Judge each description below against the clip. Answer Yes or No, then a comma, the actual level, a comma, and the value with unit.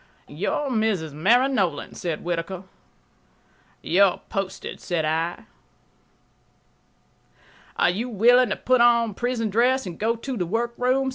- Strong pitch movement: Yes, wide, 5.7 semitones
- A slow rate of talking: Yes, slow, 125 wpm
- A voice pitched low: No, high, 220 Hz